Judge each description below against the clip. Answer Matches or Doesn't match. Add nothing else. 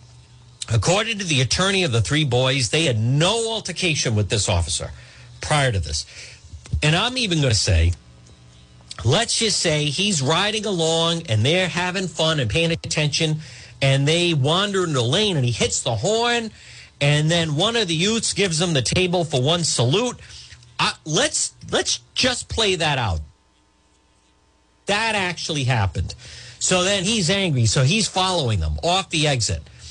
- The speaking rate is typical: Matches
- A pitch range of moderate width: Doesn't match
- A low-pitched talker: Doesn't match